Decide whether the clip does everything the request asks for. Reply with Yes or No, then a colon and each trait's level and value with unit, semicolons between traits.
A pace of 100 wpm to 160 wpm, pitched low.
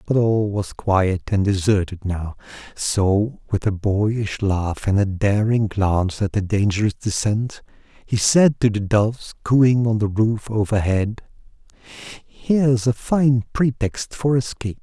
Yes: average, 145 wpm; low, 105 Hz